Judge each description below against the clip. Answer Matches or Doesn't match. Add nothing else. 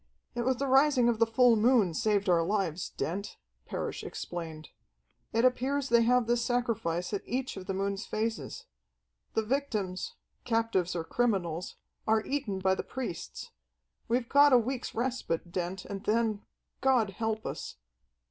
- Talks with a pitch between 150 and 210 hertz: Doesn't match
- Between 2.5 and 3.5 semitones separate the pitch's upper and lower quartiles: Doesn't match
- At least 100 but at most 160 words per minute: Matches